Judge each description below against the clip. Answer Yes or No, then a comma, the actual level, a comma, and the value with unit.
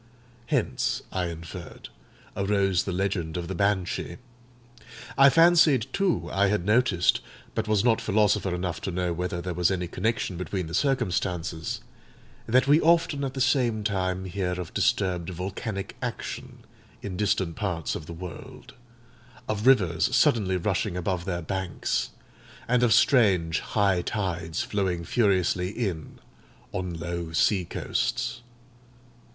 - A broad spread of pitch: No, average, 3.6 semitones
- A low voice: Yes, very low, 95 Hz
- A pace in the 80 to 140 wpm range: Yes, slow, 135 wpm